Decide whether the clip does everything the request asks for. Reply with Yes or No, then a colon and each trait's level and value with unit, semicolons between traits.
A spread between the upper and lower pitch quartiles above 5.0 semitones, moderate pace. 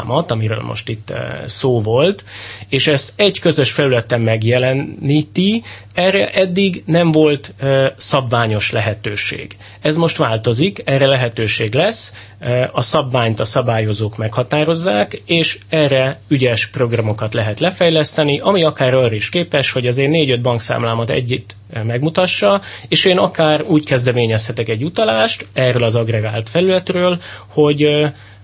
Yes: wide, 5.6 semitones; average, 135 wpm